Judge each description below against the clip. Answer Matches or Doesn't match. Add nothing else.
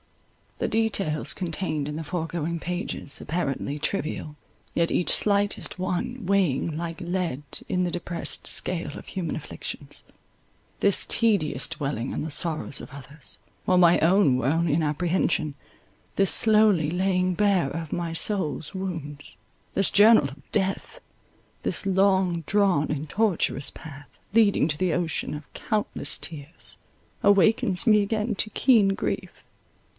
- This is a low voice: Doesn't match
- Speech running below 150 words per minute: Matches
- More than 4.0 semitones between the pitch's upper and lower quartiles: Matches